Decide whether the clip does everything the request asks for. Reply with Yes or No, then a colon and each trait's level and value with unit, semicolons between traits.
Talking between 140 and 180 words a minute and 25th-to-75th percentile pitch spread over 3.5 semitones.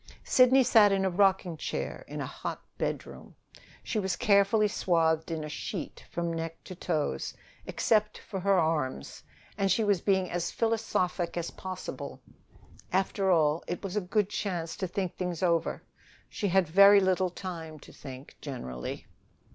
No: average, 160 wpm; average, 3.2 semitones